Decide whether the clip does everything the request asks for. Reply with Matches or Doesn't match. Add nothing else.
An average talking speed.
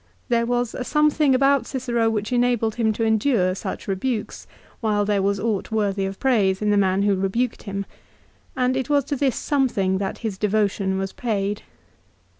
Matches